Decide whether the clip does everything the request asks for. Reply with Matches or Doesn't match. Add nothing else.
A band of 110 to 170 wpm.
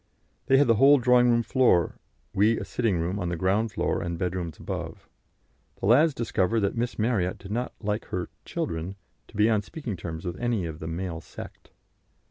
Doesn't match